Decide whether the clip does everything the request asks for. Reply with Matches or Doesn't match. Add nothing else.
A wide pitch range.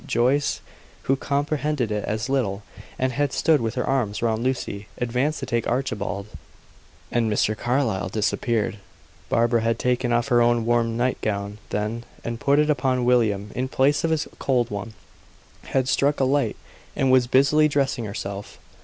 Doesn't match